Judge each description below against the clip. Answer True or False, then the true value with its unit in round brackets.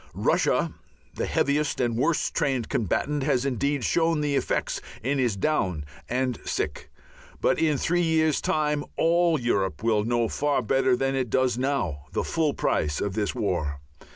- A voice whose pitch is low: True (130 Hz)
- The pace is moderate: True (160 wpm)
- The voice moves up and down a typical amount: True (4.9 semitones)